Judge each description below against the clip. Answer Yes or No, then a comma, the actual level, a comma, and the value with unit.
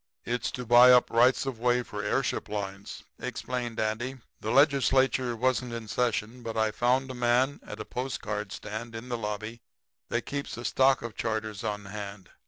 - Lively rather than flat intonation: No, average, 2.7 semitones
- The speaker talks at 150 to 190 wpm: Yes, average, 180 wpm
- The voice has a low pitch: Yes, low, 120 Hz